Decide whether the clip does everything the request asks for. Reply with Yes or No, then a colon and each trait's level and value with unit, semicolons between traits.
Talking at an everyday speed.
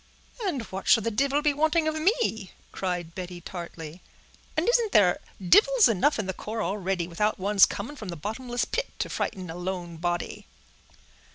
Yes: average, 175 wpm